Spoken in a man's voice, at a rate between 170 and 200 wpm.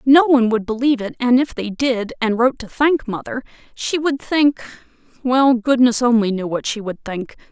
No: female; average, 190 wpm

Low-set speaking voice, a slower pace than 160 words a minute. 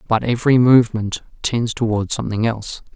Yes: low, 115 Hz; average, 140 wpm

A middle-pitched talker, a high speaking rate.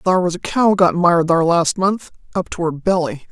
Yes: medium, 175 Hz; fast, 235 wpm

